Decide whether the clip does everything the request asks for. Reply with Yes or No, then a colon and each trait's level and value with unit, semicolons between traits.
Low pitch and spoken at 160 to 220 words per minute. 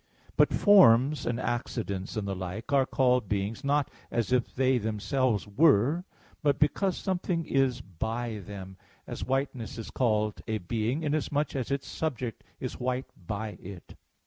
No: low, 120 Hz; average, 150 wpm